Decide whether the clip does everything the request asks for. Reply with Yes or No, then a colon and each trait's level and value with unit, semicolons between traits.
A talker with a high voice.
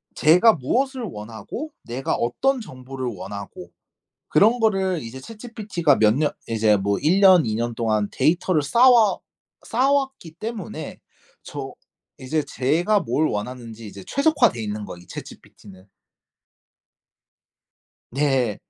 No: medium, 145 Hz